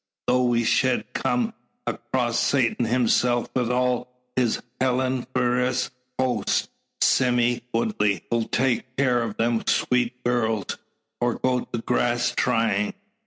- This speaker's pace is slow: Yes, slow, 120 wpm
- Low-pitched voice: Yes, low, 125 Hz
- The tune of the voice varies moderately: No, narrow, 1.4 semitones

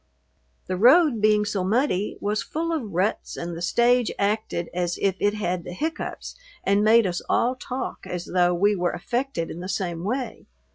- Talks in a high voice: Yes, high, 205 Hz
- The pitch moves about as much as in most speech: Yes, average, 5.0 semitones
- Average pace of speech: Yes, average, 185 wpm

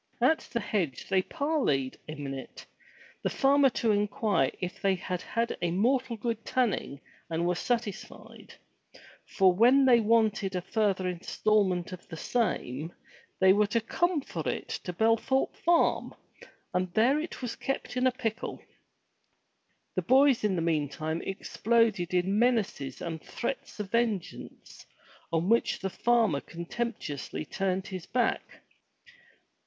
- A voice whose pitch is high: Yes, high, 205 Hz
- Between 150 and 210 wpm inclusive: No, slow, 135 wpm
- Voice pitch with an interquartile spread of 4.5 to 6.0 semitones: Yes, average, 5.1 semitones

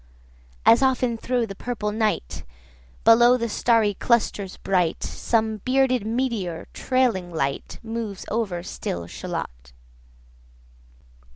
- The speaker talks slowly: Yes, slow, 110 wpm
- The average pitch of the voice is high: Yes, high, 225 Hz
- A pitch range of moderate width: Yes, average, 4.3 semitones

